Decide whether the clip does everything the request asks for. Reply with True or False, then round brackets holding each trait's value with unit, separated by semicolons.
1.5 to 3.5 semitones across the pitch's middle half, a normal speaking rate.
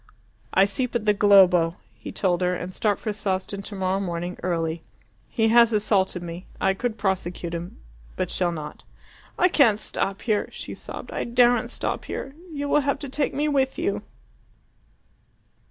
False (4.8 semitones; 170 wpm)